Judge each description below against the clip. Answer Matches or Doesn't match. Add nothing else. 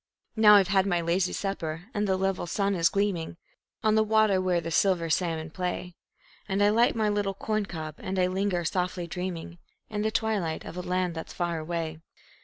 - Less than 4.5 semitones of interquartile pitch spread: Matches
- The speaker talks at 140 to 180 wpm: Doesn't match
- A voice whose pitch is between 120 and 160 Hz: Doesn't match